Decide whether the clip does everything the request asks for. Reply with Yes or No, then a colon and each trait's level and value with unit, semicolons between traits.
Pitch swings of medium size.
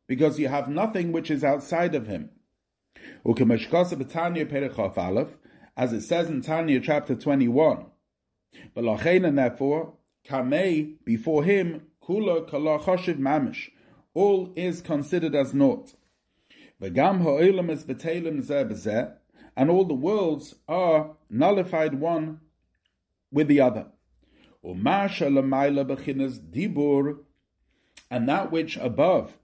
Yes: average, 3.4 semitones